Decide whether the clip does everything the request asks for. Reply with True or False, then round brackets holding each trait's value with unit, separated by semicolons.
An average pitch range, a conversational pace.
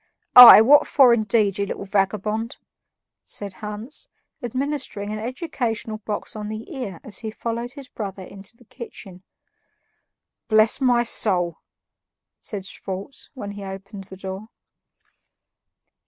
False (3.3 semitones; 125 wpm)